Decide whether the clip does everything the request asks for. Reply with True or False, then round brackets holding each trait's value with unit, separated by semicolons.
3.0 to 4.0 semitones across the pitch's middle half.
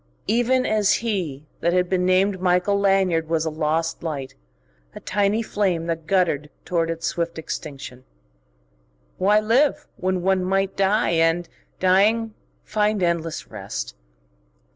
True (3.6 semitones)